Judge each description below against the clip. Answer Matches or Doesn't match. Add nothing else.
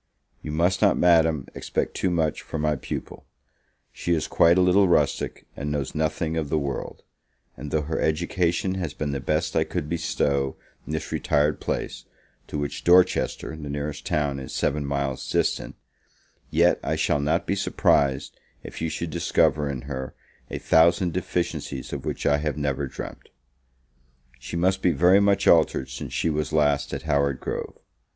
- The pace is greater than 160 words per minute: Matches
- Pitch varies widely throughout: Doesn't match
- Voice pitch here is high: Doesn't match